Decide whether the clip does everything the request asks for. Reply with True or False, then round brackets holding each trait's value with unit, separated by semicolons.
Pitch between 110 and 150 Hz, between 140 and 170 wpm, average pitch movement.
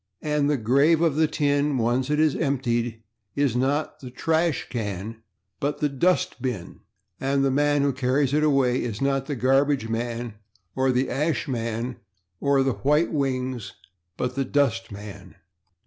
True (135 Hz; 160 wpm; 3.1 semitones)